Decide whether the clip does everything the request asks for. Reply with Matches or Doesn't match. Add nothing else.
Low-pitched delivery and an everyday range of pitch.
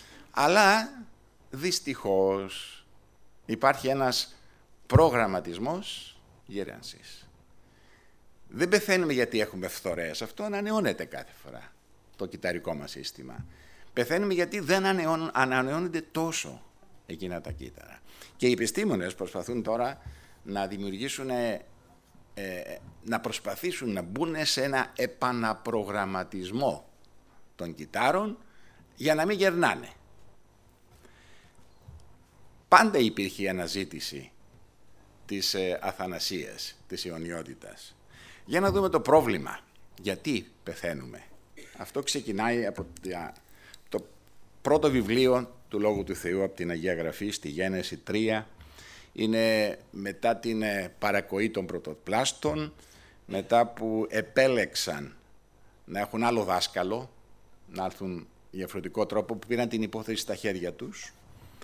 Doesn't match